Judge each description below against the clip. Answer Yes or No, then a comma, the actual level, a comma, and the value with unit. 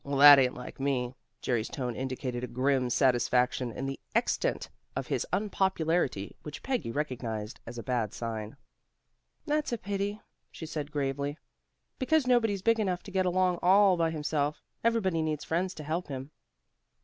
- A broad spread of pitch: Yes, wide, 6.6 semitones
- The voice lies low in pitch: No, medium, 145 Hz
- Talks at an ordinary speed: Yes, average, 160 wpm